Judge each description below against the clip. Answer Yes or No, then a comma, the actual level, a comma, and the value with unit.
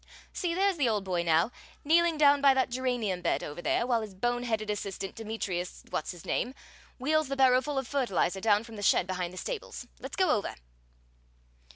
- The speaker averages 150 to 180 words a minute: No, average, 195 wpm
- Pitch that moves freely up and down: Yes, wide, 6.3 semitones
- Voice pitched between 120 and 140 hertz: No, high, 235 Hz